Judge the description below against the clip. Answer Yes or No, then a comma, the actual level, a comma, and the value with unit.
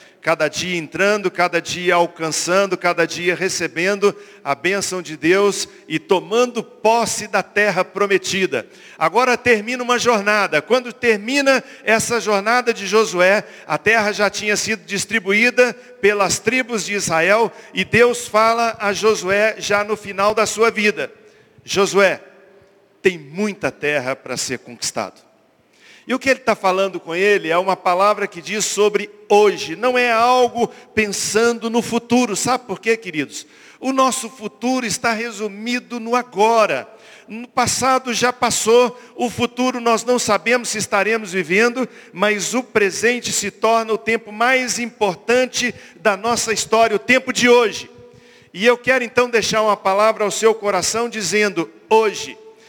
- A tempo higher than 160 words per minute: No, average, 145 wpm